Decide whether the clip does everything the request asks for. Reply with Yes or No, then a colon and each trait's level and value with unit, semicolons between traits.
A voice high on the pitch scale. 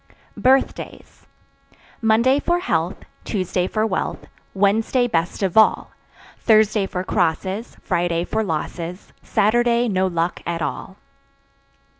Yes: high, 200 Hz